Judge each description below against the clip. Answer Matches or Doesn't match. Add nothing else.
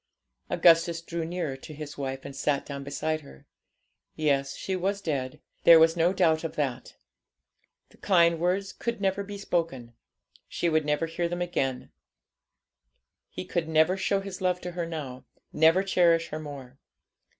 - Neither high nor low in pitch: Matches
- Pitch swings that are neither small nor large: Matches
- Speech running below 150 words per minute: Doesn't match